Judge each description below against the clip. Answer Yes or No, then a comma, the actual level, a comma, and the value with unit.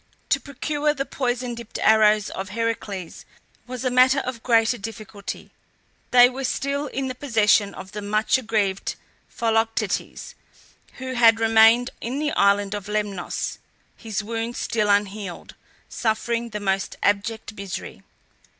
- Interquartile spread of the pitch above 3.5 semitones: No, average, 3.1 semitones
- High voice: Yes, high, 225 Hz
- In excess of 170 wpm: No, slow, 135 wpm